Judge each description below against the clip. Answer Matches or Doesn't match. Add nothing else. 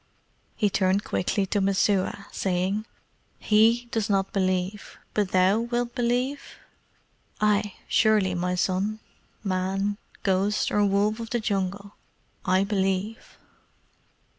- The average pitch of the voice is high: Matches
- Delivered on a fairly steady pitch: Matches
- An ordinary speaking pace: Doesn't match